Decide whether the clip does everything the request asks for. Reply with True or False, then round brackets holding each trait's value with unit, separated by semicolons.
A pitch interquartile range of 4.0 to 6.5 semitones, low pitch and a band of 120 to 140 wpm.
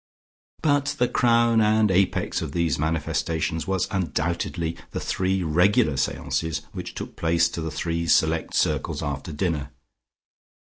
False (3.6 semitones; 85 Hz; 135 wpm)